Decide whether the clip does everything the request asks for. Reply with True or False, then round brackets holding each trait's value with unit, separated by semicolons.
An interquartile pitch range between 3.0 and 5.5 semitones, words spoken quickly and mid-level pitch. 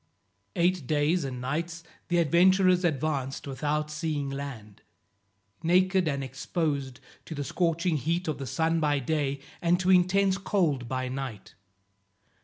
False (4.2 semitones; 135 wpm; 155 Hz)